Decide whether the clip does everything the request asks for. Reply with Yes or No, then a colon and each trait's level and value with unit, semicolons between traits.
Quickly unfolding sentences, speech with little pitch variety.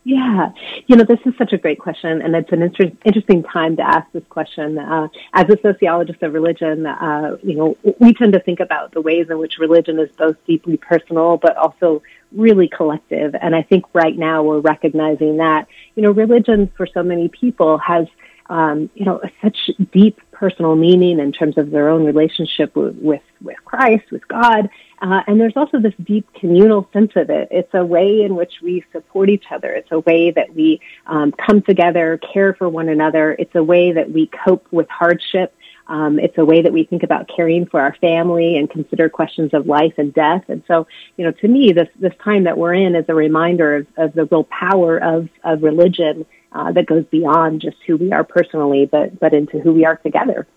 No: fast, 210 wpm; average, 3.2 semitones